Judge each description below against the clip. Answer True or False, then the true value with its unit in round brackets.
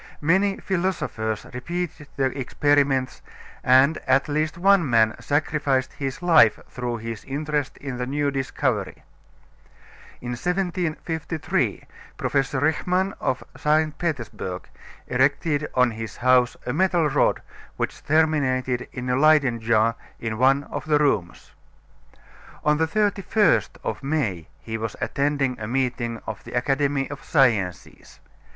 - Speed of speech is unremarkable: False (125 wpm)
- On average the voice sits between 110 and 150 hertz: True (140 Hz)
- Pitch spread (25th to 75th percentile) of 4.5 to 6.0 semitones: False (4.0 semitones)